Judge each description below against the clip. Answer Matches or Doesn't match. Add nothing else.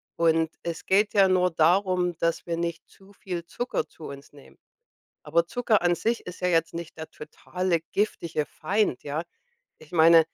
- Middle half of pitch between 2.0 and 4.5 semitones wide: Matches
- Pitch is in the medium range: Matches